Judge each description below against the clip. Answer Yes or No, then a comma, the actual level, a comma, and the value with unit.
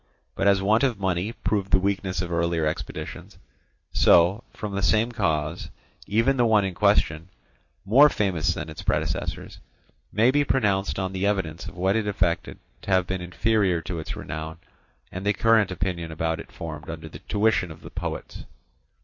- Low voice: Yes, very low, 95 Hz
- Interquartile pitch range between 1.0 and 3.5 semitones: No, average, 3.9 semitones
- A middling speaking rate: Yes, average, 180 wpm